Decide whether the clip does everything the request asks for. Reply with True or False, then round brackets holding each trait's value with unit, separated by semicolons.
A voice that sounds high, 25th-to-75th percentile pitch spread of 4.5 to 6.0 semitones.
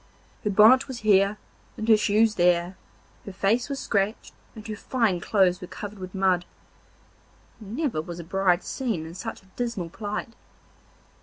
False (205 Hz; 3.5 semitones)